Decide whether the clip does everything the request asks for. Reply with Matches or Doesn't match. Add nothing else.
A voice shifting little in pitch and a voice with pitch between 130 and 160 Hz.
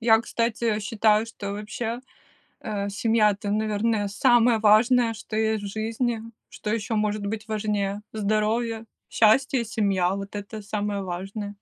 Doesn't match